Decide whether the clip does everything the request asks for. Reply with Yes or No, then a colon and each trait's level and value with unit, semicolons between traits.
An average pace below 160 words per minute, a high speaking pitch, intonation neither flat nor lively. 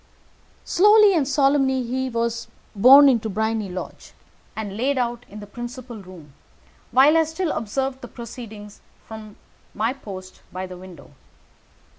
Yes: average, 140 wpm; high, 235 Hz; average, 4.4 semitones